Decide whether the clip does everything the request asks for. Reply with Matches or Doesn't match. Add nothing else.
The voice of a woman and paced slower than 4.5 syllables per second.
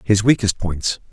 Doesn't match